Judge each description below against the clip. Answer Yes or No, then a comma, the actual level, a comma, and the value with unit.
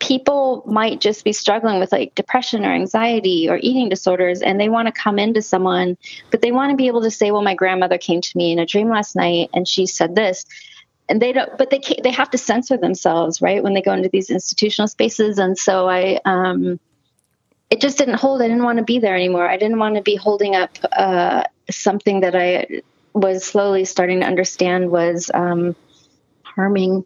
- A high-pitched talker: Yes, high, 200 Hz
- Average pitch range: Yes, average, 3.6 semitones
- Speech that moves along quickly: Yes, fast, 215 wpm